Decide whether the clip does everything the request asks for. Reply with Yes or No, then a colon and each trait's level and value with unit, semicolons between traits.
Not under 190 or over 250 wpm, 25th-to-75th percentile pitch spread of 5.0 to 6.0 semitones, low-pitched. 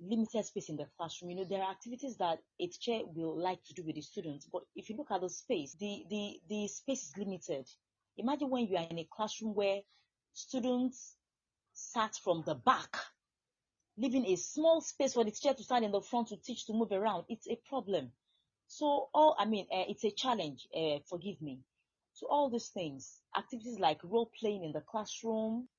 No: fast, 205 wpm; wide, 5.4 semitones; high, 210 Hz